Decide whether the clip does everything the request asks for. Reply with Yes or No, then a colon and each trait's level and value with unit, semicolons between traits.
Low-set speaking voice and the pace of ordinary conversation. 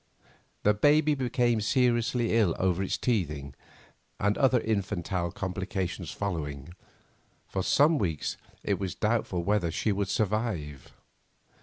No: low, 100 Hz; slow, 120 wpm